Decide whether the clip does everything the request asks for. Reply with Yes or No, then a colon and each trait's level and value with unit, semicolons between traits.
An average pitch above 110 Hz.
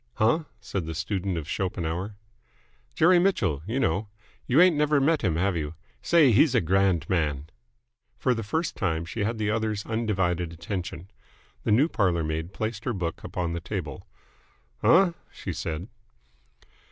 No: low, 100 Hz